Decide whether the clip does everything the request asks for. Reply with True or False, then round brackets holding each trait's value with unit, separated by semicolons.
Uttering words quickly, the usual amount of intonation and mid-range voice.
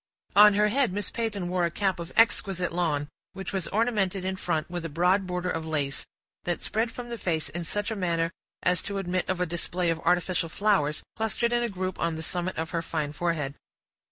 True (215 wpm; 3.4 semitones; 180 Hz)